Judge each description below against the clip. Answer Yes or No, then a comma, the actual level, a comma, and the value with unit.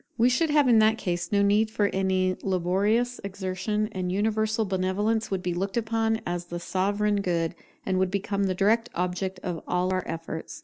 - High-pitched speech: Yes, high, 195 Hz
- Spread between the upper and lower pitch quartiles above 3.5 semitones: No, average, 3.0 semitones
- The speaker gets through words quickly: No, average, 185 wpm